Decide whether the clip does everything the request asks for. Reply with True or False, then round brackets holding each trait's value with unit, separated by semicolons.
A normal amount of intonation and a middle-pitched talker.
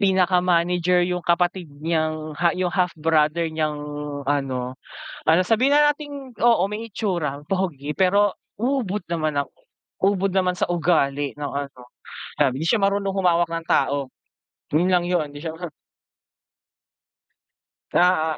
True (3.6 semitones; 175 Hz)